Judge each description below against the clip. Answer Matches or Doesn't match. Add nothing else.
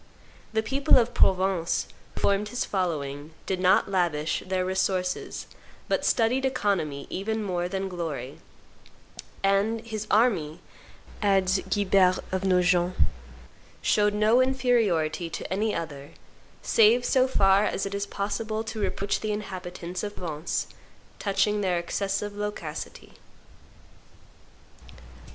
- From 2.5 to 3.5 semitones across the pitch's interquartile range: Matches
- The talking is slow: Matches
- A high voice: Matches